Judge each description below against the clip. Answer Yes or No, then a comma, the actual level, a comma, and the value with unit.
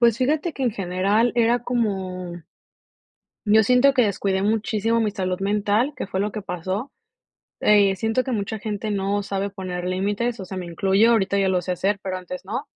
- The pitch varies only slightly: No, average, 3.1 semitones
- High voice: Yes, high, 205 Hz